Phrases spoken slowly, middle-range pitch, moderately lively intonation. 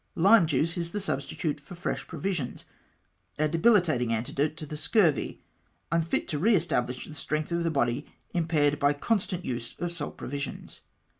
No: average, 170 wpm; medium, 155 Hz; average, 3.2 semitones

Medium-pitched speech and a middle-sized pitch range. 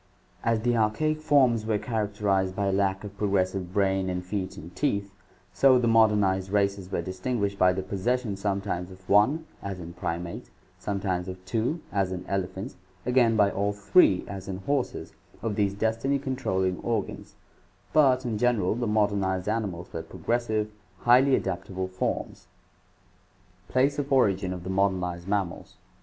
No: low, 100 Hz; average, 3.5 semitones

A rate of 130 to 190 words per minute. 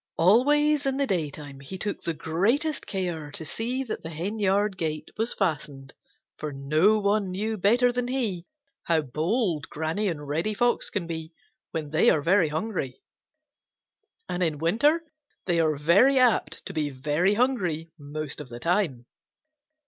Yes: average, 155 wpm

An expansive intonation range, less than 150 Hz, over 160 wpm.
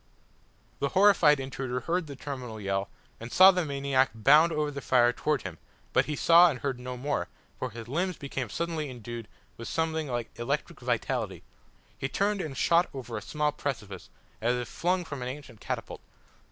No: average, 4.6 semitones; low, 135 Hz; average, 180 wpm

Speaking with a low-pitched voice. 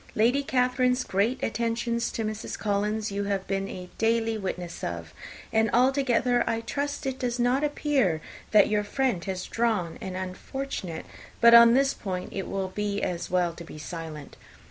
No: high, 215 Hz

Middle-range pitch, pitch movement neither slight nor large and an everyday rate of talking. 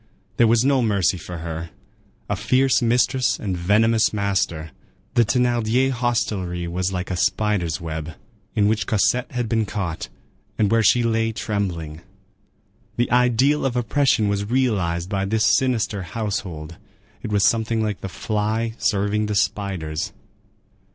No: low, 105 Hz; average, 4.2 semitones; average, 145 wpm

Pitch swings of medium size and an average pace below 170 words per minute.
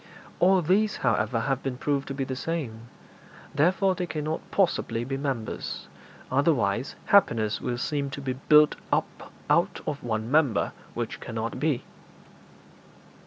Yes: average, 4.5 semitones; average, 140 wpm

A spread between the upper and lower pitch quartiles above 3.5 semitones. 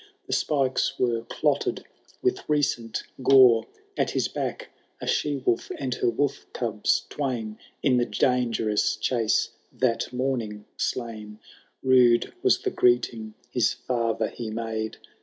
No: average, 2.7 semitones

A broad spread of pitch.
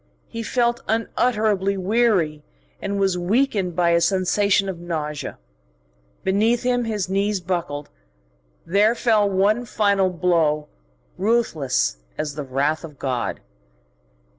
No: average, 4.6 semitones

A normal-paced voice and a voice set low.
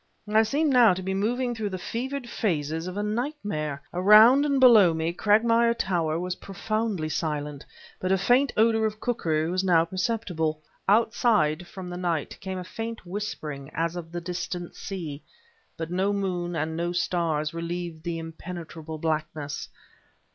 No: average, 160 wpm; medium, 180 Hz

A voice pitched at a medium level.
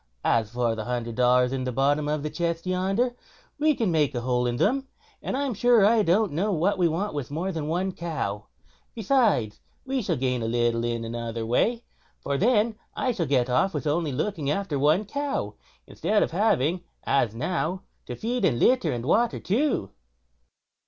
Yes: medium, 160 Hz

